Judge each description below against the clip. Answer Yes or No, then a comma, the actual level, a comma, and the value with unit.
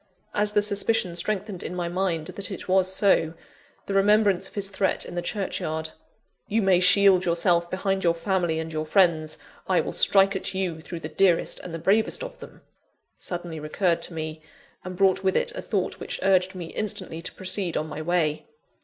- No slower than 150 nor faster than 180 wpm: No, average, 200 wpm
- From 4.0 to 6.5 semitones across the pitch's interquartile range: No, average, 2.7 semitones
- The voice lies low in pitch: No, medium, 185 Hz